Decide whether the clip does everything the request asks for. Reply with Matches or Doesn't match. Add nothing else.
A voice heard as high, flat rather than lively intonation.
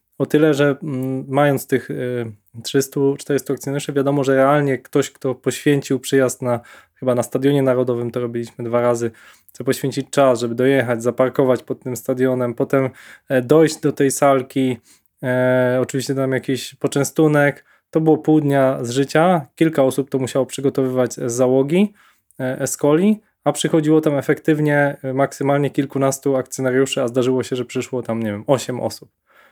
Doesn't match